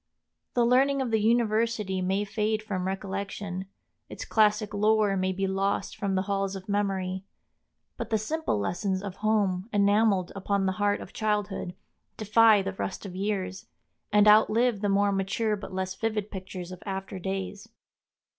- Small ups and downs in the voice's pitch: Yes, narrow, 2.0 semitones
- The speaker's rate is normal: Yes, average, 160 wpm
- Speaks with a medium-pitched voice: No, high, 200 Hz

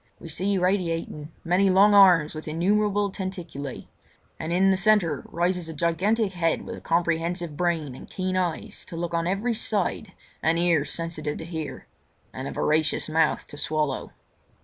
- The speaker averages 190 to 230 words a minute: No, average, 160 wpm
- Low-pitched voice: No, medium, 170 Hz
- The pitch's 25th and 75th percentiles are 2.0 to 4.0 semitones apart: Yes, average, 3.0 semitones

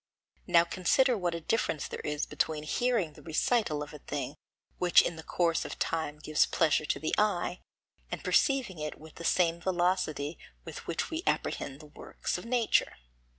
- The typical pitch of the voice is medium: Yes, medium, 170 Hz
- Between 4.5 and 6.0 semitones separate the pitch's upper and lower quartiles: No, average, 3.6 semitones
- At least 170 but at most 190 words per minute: Yes, average, 180 wpm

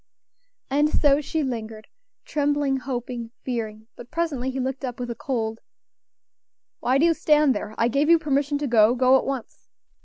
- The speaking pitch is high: Yes, very high, 265 Hz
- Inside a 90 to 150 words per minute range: No, average, 175 wpm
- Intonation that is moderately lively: Yes, average, 3.4 semitones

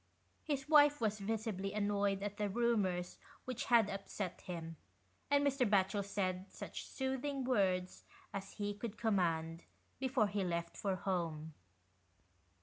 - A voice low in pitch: No, high, 205 Hz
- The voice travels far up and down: No, average, 4.2 semitones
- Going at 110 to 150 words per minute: Yes, slow, 135 wpm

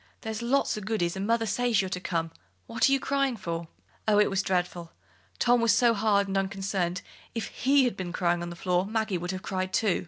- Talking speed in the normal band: No, fast, 225 wpm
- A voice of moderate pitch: No, high, 195 Hz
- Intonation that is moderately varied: Yes, average, 3.9 semitones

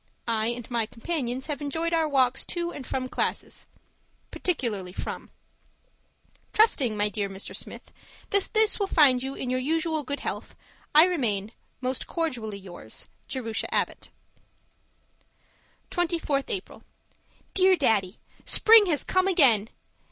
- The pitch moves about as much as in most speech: No, wide, 6.7 semitones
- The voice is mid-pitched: No, very high, 270 Hz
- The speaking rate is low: Yes, slow, 130 wpm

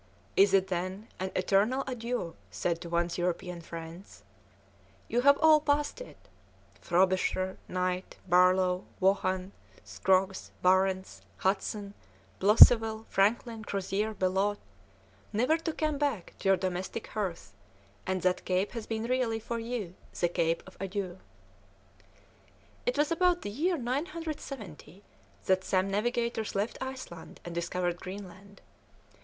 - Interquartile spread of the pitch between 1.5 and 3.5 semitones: No, average, 4.3 semitones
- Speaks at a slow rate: Yes, slow, 125 wpm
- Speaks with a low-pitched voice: No, high, 195 Hz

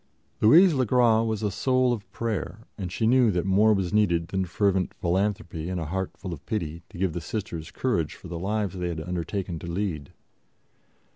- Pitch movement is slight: No, average, 4.1 semitones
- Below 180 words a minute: No, average, 200 wpm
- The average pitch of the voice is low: Yes, very low, 95 Hz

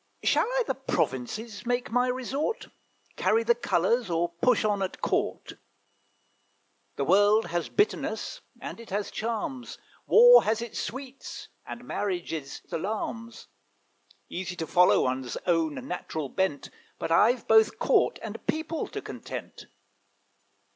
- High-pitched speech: Yes, high, 220 Hz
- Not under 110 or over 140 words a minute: Yes, slow, 135 wpm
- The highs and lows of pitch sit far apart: Yes, wide, 6.4 semitones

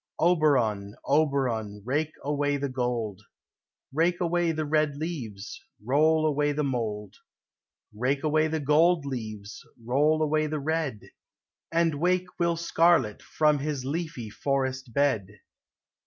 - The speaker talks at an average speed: No, slow, 125 wpm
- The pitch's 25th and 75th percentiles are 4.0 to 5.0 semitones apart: Yes, average, 4.3 semitones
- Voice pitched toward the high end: No, medium, 145 Hz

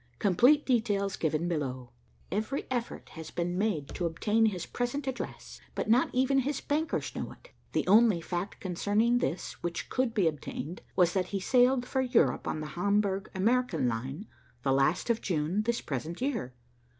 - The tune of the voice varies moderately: No, wide, 6.4 semitones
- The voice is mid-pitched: No, high, 200 Hz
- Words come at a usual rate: Yes, average, 170 wpm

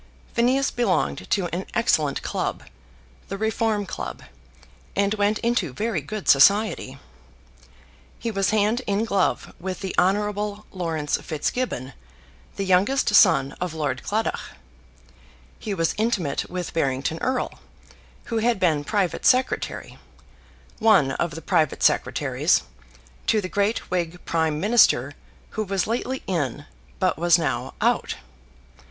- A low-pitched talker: No, high, 195 Hz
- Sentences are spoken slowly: Yes, slow, 125 wpm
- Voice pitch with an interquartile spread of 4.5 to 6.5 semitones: Yes, average, 5.2 semitones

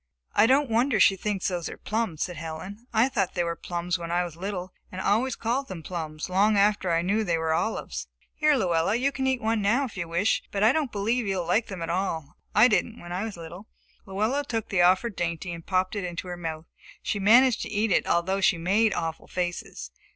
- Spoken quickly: Yes, fast, 230 wpm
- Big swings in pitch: No, average, 4.3 semitones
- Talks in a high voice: Yes, high, 195 Hz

